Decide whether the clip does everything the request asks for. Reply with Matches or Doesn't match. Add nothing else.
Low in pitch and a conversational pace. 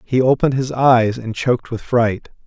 Matches